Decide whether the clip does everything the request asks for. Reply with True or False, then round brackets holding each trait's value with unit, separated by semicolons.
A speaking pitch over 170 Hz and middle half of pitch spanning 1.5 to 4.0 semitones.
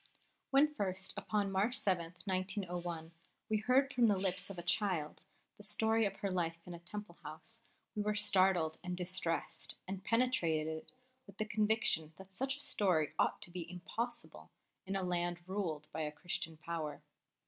True (185 Hz; 3.7 semitones)